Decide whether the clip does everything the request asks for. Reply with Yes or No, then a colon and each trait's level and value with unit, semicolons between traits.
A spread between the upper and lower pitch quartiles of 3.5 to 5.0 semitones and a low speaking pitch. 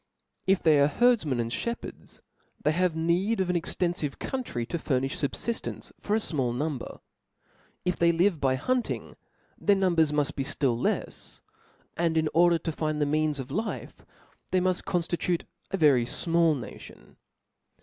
No: average, 4.1 semitones; medium, 165 Hz